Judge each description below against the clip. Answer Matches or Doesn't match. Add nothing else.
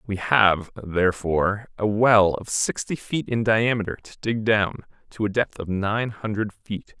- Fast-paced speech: Doesn't match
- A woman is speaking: Doesn't match